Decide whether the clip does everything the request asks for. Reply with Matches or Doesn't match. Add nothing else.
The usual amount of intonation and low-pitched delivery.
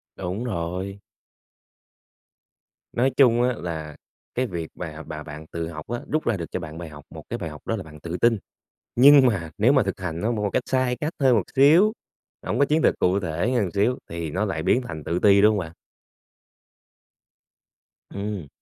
Doesn't match